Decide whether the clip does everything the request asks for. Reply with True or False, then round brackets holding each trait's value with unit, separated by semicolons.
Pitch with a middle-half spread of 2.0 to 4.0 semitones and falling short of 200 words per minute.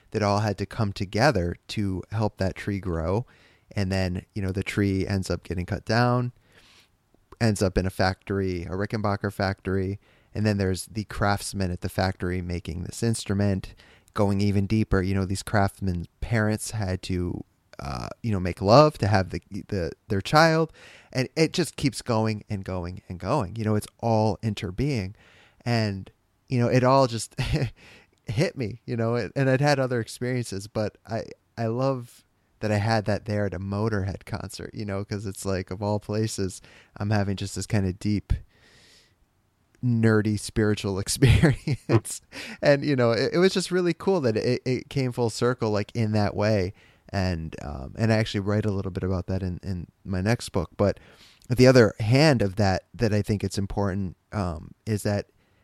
True (3.3 semitones; 185 wpm)